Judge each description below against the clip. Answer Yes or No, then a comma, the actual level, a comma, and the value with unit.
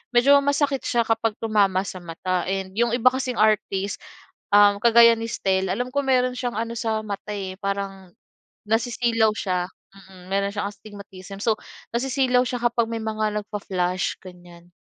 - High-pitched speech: Yes, high, 215 Hz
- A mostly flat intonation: No, average, 3.6 semitones